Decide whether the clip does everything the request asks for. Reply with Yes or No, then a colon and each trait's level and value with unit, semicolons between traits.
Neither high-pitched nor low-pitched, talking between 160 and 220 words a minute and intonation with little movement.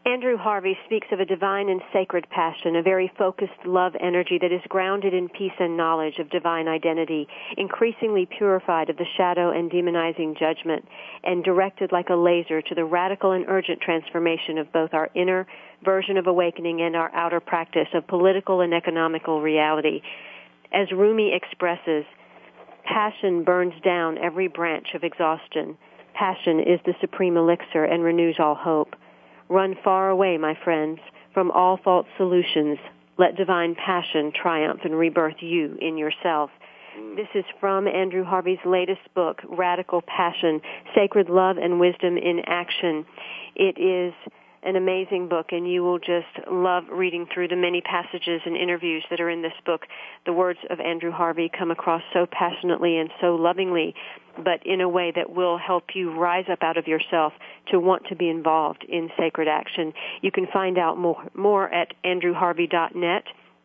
Yes: medium, 175 Hz; average, 165 wpm; narrow, 1.9 semitones